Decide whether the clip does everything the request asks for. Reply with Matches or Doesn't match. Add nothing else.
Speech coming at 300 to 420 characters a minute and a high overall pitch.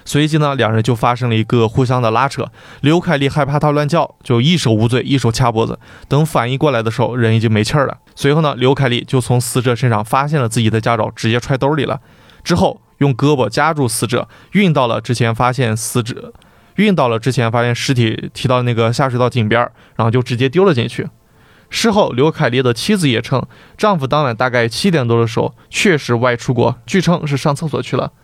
Doesn't match